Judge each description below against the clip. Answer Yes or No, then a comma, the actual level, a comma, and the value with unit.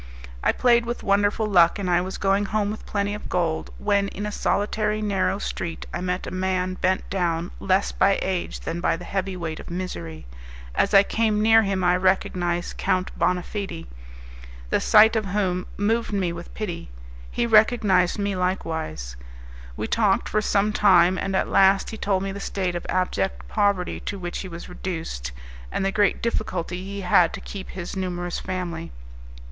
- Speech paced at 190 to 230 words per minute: No, average, 180 wpm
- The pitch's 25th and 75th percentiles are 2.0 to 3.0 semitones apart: Yes, narrow, 2.5 semitones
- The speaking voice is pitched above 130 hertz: Yes, high, 190 Hz